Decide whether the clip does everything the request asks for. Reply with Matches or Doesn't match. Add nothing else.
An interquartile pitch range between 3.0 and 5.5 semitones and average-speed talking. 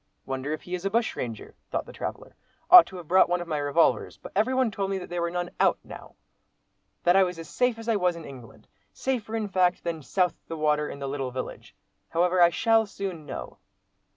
Doesn't match